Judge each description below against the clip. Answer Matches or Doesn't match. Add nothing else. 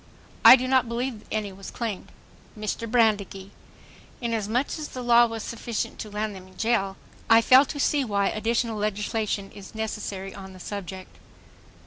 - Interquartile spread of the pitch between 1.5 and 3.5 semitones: Matches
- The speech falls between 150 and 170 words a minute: Matches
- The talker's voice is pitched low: Doesn't match